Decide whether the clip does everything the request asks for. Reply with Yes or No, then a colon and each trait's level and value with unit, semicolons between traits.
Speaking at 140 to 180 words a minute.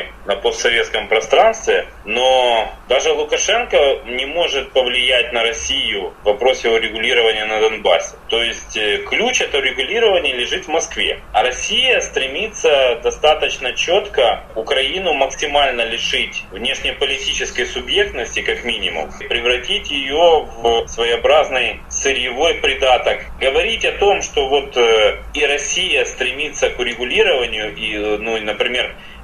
No: average, 115 wpm